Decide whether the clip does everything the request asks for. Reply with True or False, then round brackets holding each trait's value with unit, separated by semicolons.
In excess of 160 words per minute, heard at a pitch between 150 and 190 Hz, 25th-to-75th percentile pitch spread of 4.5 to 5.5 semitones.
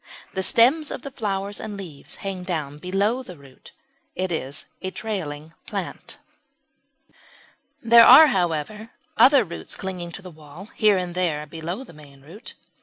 False (155 wpm; 185 Hz; 5.2 semitones)